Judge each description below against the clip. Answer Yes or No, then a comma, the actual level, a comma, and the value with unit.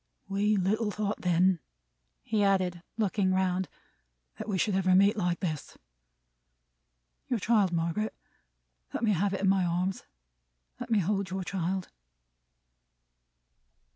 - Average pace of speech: No, slow, 130 wpm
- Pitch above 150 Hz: Yes, high, 190 Hz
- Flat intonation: Yes, narrow, 2.2 semitones